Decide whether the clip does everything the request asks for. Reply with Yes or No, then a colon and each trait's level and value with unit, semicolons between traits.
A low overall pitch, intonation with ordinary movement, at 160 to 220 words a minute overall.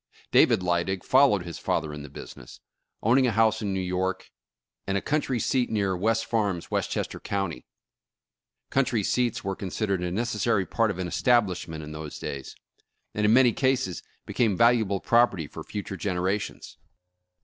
Yes: low, 100 Hz; average, 4.4 semitones; average, 165 wpm